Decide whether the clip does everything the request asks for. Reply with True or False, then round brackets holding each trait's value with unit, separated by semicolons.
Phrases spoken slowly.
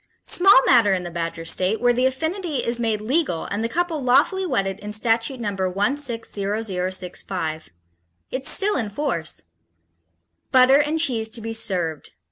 False (150 wpm)